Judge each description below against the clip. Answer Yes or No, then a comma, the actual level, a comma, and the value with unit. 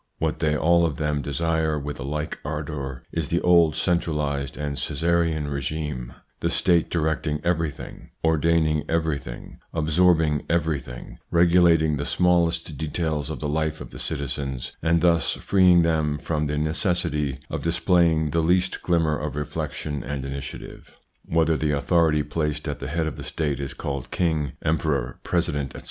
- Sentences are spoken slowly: No, average, 155 wpm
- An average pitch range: No, narrow, 2.3 semitones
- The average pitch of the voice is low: Yes, very low, 80 Hz